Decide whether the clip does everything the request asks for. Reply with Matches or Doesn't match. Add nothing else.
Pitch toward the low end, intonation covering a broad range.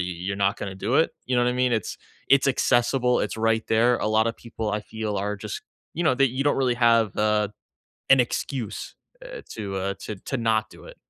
Doesn't match